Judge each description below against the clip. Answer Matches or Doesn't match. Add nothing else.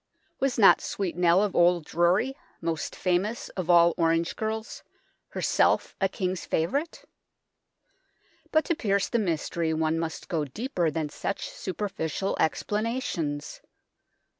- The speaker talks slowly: Matches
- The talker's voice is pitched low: Doesn't match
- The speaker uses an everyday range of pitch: Matches